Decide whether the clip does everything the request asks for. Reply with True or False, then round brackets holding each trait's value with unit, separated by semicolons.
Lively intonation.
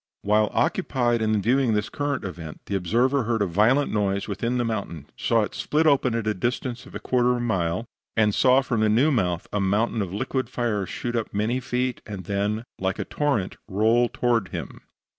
False (3.3 semitones)